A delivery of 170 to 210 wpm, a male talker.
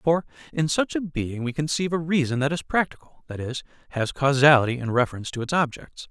Yes: fast, 205 wpm; male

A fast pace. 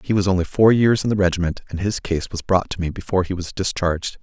Yes: fast, 270 wpm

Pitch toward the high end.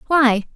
Yes: very high, 260 Hz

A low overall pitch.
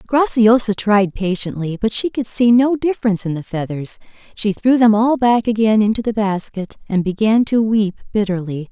No: high, 215 Hz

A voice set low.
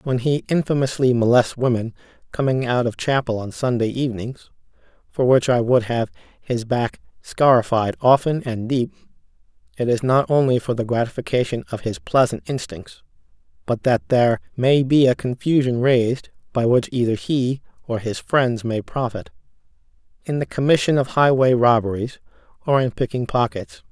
Yes: low, 125 Hz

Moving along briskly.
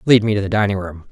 Yes: fast, 325 wpm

